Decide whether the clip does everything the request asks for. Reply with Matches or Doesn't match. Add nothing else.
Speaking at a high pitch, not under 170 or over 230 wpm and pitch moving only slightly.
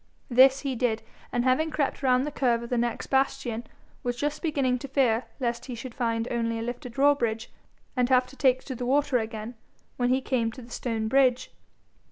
Matches